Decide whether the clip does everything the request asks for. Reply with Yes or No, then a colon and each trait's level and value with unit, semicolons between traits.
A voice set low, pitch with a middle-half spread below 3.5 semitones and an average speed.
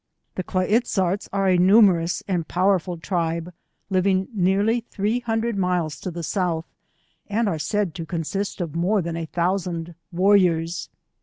No: medium, 185 Hz; average, 2.9 semitones; average, 160 wpm